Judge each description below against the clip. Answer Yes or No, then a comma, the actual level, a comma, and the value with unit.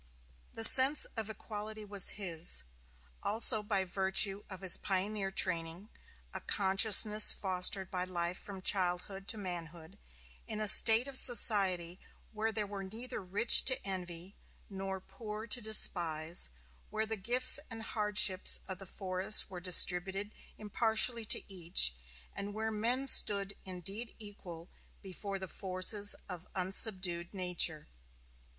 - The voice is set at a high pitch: Yes, high, 195 Hz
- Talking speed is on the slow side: Yes, slow, 130 wpm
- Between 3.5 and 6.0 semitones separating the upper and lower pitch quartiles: No, average, 2.8 semitones